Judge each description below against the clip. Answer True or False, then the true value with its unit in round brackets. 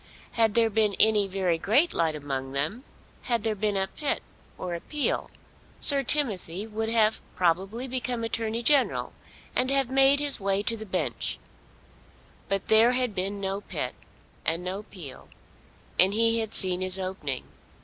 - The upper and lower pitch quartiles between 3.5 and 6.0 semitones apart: True (4.0 semitones)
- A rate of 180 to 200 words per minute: False (160 wpm)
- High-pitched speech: True (210 Hz)